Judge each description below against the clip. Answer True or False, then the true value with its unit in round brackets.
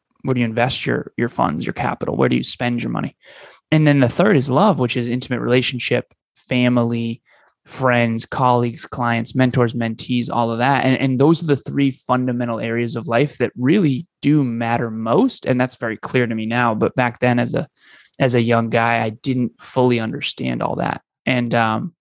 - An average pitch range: False (2.0 semitones)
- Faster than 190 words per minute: True (200 wpm)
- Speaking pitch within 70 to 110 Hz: False (120 Hz)